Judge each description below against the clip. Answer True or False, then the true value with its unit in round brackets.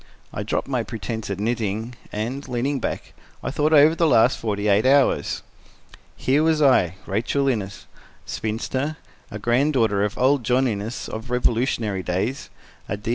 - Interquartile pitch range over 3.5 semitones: True (4.3 semitones)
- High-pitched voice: False (120 Hz)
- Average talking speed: True (155 wpm)